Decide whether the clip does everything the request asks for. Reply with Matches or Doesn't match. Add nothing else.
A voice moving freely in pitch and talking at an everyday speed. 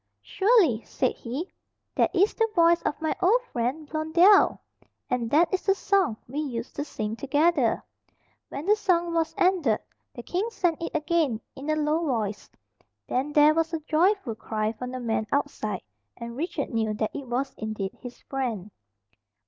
Matches